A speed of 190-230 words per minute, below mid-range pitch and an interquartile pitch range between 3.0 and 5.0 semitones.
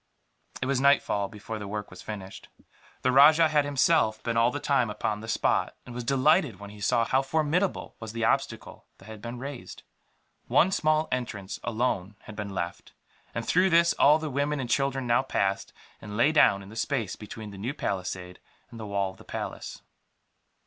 No: average, 195 wpm; low, 120 Hz; wide, 5.4 semitones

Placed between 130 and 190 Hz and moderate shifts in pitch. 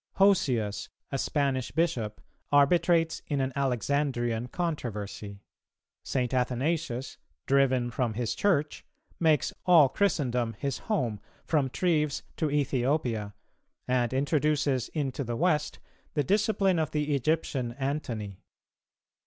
Yes: medium, 140 Hz; average, 4.0 semitones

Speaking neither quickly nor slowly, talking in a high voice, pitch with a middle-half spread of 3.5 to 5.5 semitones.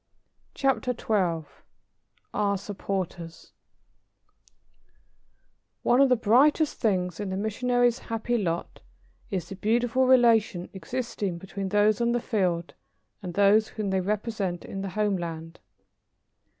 No: slow, 115 wpm; high, 205 Hz; average, 4.2 semitones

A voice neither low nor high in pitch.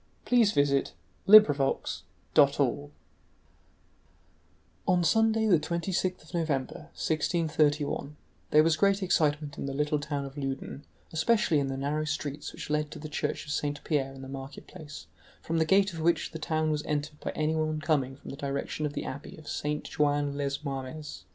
Yes: medium, 150 Hz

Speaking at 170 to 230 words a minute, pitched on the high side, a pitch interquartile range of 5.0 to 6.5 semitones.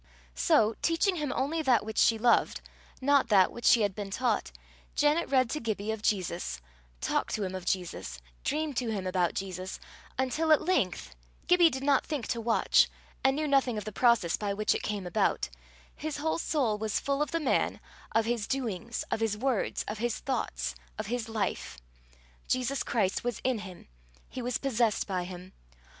Yes: average, 185 wpm; high, 230 Hz; wide, 5.4 semitones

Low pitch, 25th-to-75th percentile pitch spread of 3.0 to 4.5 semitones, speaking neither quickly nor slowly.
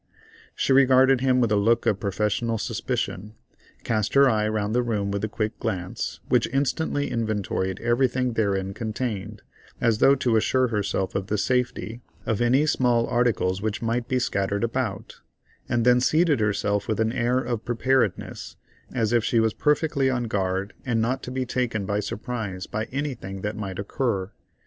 Yes: low, 115 Hz; average, 3.5 semitones; average, 170 wpm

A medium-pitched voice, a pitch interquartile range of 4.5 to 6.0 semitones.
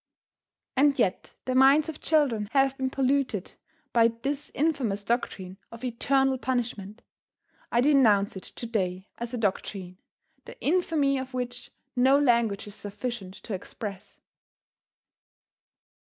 No: high, 245 Hz; average, 4.8 semitones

